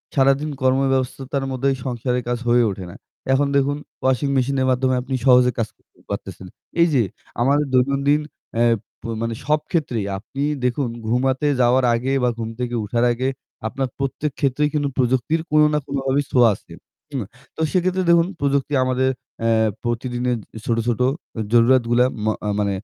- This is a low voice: Yes, low, 130 Hz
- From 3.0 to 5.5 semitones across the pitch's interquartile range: No, narrow, 2.4 semitones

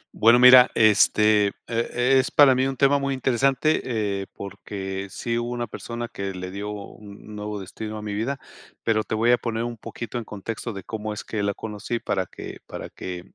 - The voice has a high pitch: No, low, 110 Hz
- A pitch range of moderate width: Yes, average, 3.0 semitones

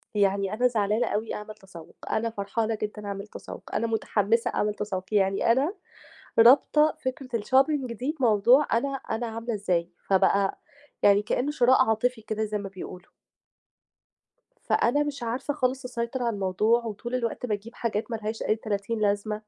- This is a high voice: Yes, high, 225 Hz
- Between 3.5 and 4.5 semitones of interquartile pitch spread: No, average, 3.1 semitones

